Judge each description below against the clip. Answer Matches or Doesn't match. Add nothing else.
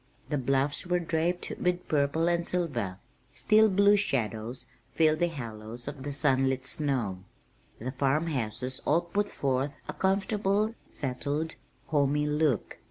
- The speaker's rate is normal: Doesn't match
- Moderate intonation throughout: Matches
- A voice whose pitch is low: Doesn't match